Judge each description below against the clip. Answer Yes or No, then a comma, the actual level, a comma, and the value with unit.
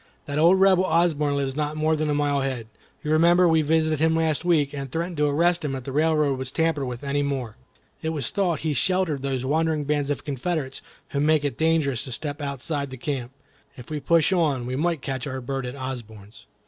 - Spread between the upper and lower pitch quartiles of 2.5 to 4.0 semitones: Yes, average, 3.1 semitones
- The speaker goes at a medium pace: No, fast, 220 wpm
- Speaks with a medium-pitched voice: Yes, medium, 145 Hz